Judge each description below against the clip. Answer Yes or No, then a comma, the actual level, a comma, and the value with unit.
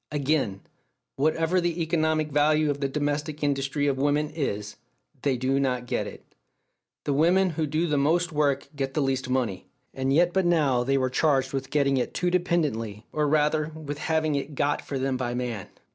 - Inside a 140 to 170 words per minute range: No, average, 190 wpm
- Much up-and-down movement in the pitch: No, average, 2.8 semitones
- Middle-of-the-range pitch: Yes, medium, 145 Hz